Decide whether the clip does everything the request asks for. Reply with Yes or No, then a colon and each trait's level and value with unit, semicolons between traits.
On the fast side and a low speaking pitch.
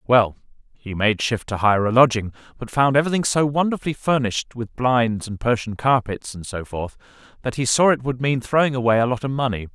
Yes: fast, 210 wpm; low, 120 Hz